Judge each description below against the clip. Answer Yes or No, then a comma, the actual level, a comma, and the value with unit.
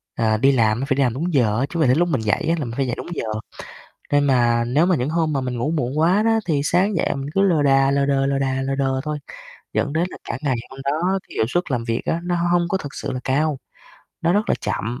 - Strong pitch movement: No, average, 4.3 semitones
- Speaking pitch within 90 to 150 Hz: Yes, medium, 140 Hz